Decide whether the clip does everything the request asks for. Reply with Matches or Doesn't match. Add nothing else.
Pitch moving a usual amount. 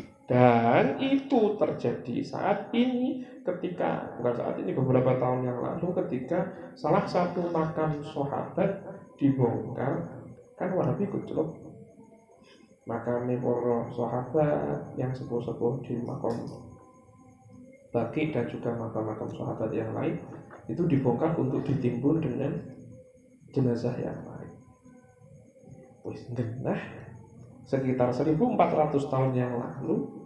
Matches